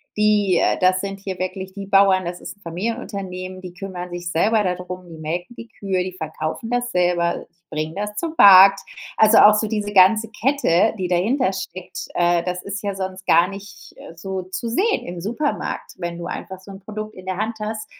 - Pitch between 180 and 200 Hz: Yes, high, 190 Hz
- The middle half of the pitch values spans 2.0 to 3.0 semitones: Yes, average, 2.7 semitones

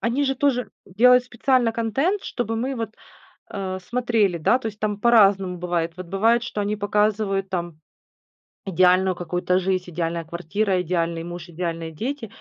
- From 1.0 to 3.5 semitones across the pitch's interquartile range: No, average, 4.7 semitones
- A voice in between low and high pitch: No, high, 195 Hz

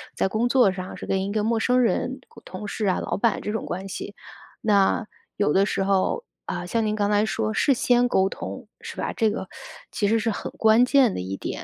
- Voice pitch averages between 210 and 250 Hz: Yes, high, 215 Hz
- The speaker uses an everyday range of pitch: Yes, average, 3.1 semitones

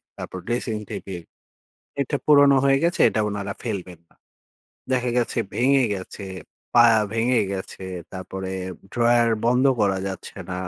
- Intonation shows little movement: No, average, 4.6 semitones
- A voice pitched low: Yes, low, 115 Hz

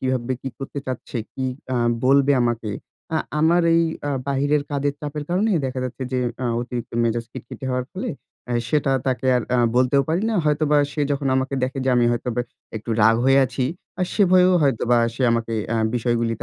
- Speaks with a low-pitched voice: Yes, low, 130 Hz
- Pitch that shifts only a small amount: No, average, 3.2 semitones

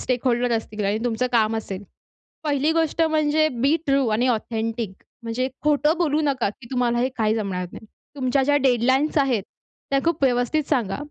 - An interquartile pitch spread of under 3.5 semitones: No, average, 4.2 semitones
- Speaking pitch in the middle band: No, very high, 250 Hz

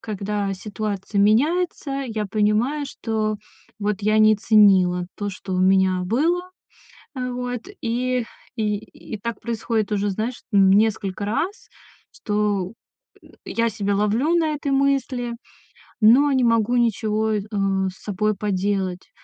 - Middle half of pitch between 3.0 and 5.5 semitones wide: Yes, average, 3.3 semitones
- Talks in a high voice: Yes, high, 215 Hz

